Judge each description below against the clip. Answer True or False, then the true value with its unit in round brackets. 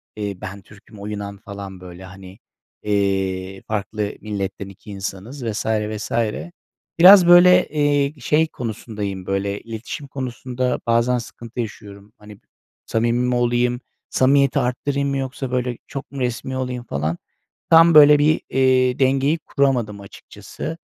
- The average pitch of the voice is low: True (115 Hz)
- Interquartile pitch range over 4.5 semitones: True (4.9 semitones)